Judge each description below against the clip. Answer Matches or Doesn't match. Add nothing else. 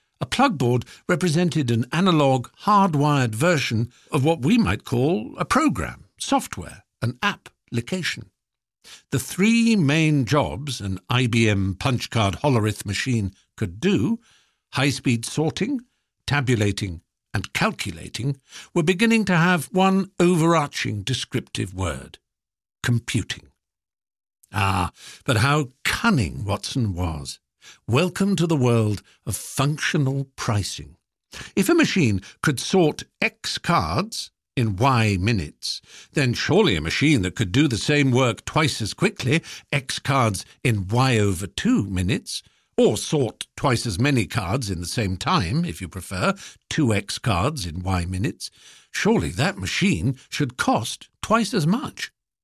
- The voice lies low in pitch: Matches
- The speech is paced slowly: Matches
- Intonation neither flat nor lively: Doesn't match